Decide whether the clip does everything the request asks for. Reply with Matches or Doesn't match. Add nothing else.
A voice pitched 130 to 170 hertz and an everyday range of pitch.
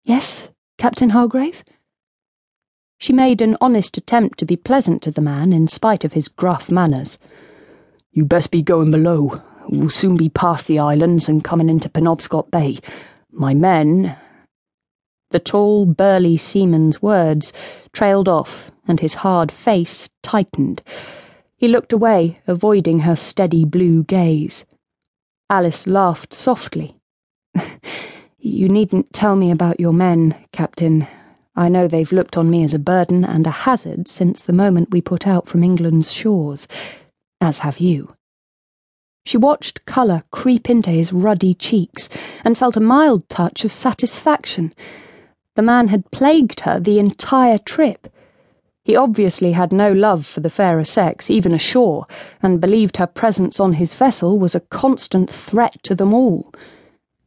Doesn't match